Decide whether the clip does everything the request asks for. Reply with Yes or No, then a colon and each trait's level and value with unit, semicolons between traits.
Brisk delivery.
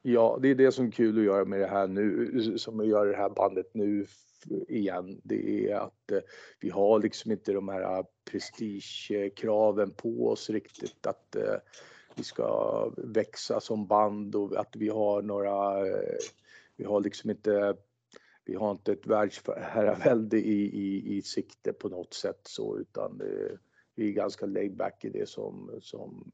No: average, 165 wpm